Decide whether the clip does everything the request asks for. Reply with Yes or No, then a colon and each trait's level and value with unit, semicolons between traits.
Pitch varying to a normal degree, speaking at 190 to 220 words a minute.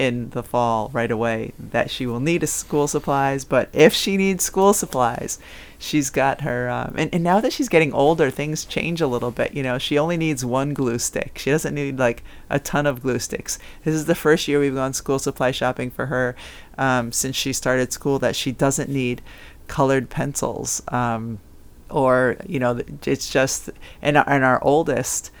Yes: average, 3.5 semitones; average, 195 wpm